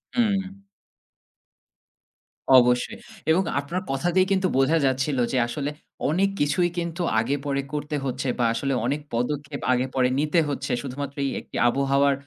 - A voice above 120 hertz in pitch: Yes, medium, 140 Hz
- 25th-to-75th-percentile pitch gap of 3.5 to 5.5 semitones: Yes, average, 3.9 semitones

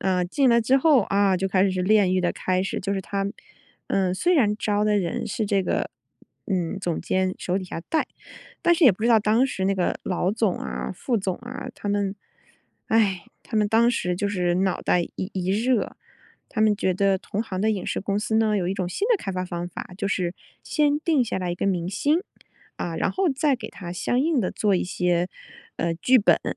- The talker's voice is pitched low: No, high, 200 Hz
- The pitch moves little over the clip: No, average, 3.5 semitones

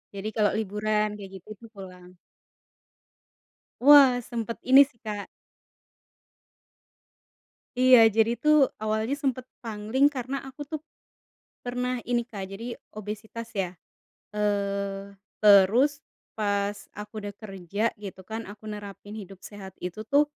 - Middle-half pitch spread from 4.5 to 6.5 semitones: No, average, 3.5 semitones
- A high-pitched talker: Yes, high, 215 Hz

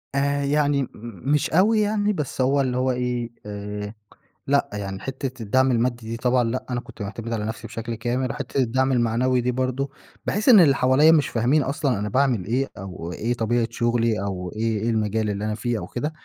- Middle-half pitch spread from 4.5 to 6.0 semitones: No, average, 3.4 semitones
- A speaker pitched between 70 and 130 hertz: Yes, low, 125 Hz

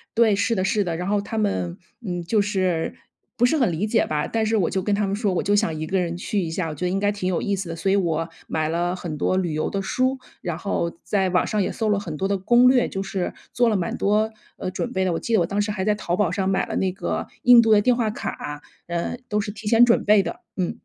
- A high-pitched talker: Yes, high, 195 Hz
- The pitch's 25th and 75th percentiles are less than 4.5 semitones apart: Yes, average, 3.3 semitones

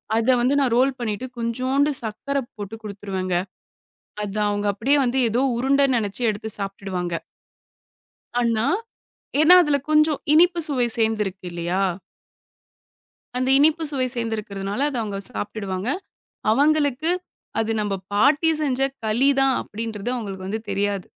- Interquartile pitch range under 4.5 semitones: No, average, 5.1 semitones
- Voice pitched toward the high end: Yes, high, 225 Hz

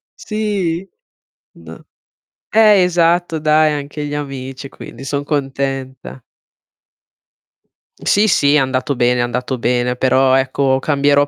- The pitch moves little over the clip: No, average, 3.2 semitones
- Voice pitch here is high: No, medium, 140 Hz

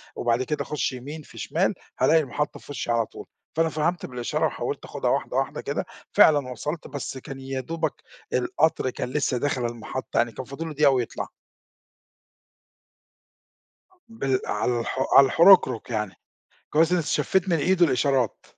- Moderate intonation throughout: Yes, average, 4.1 semitones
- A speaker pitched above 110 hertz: Yes, low, 135 Hz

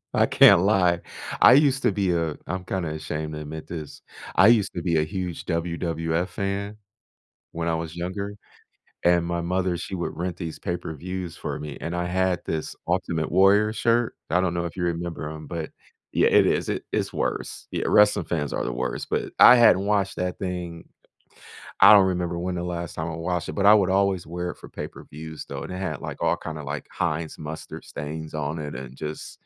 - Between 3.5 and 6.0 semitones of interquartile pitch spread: No, average, 2.8 semitones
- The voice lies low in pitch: Yes, very low, 85 Hz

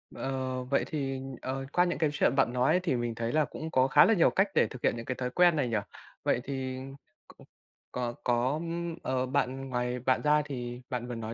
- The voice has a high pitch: No, low, 130 Hz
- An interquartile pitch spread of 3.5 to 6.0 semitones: No, narrow, 2.5 semitones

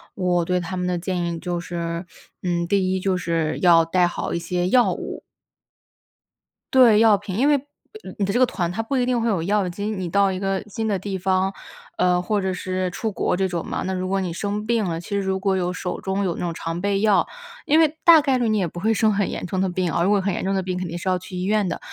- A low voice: No, high, 190 Hz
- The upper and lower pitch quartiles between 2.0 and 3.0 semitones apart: Yes, narrow, 2.5 semitones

